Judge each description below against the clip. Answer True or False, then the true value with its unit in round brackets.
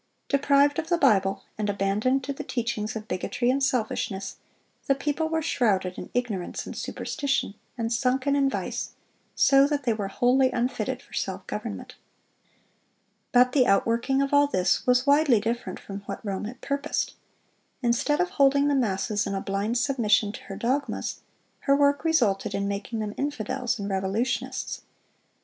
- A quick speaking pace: False (165 wpm)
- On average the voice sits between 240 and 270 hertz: True (245 Hz)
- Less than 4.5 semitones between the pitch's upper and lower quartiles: False (5.1 semitones)